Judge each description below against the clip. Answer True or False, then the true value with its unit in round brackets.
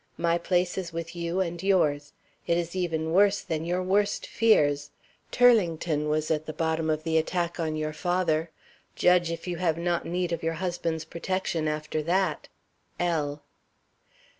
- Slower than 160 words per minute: False (165 wpm)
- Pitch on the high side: False (170 Hz)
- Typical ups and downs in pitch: False (2.2 semitones)